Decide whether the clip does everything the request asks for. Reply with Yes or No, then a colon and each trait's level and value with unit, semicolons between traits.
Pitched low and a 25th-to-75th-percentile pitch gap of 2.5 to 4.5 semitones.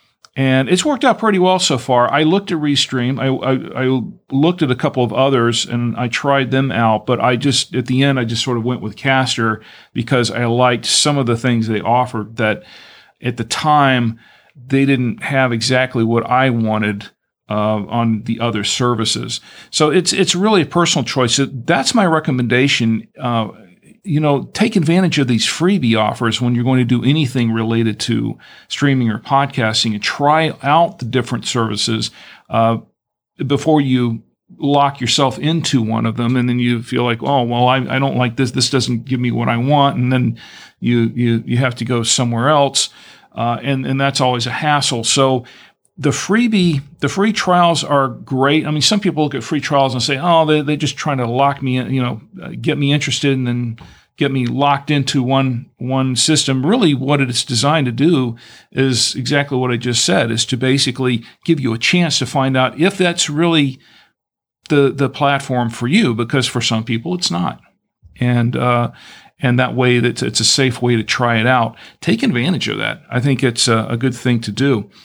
Yes: low, 130 Hz; average, 3.1 semitones